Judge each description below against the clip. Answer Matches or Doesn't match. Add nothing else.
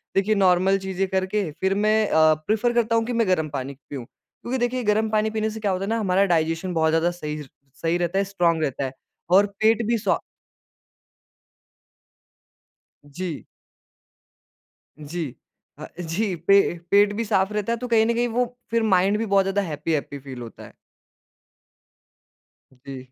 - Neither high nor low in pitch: Doesn't match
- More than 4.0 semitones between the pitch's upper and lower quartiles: Matches